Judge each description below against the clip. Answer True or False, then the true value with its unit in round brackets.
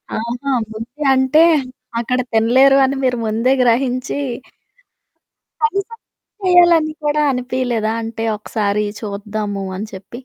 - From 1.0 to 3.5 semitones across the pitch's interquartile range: False (4.0 semitones)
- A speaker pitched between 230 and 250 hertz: True (245 Hz)